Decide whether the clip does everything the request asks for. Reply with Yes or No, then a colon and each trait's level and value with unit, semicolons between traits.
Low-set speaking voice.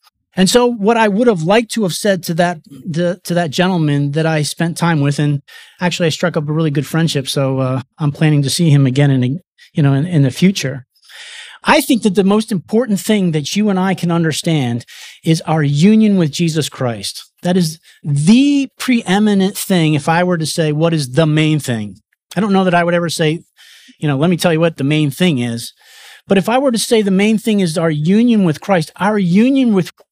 No: medium, 170 Hz